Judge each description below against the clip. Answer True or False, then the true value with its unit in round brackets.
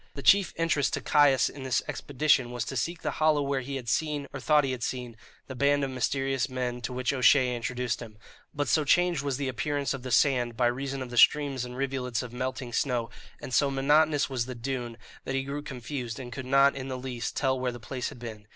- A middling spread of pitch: False (2.3 semitones)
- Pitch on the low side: True (130 Hz)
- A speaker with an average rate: False (235 wpm)